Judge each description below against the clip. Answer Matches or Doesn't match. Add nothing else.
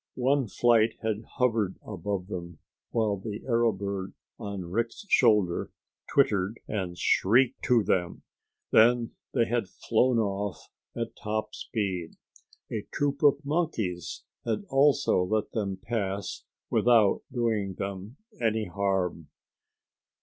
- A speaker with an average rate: Doesn't match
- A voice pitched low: Matches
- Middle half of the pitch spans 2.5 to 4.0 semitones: Matches